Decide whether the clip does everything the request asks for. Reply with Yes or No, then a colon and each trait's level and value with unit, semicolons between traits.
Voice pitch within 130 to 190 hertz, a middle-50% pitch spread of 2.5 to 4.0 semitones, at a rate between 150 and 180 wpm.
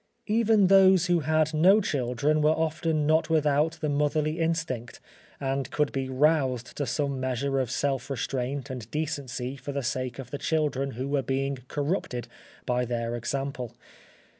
Yes: medium, 140 Hz; average, 3.3 semitones; average, 160 wpm